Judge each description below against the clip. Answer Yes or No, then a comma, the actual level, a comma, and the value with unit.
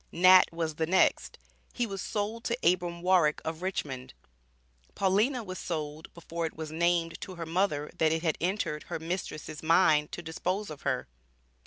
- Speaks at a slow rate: No, average, 170 wpm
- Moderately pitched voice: Yes, medium, 170 Hz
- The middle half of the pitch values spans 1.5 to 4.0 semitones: Yes, average, 2.9 semitones